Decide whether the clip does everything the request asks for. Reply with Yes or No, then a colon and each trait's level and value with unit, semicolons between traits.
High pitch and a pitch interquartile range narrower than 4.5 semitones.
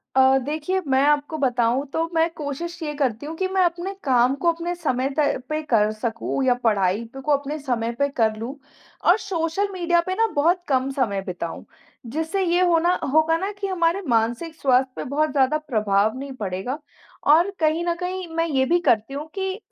No: very high, 290 Hz; average, 5.2 semitones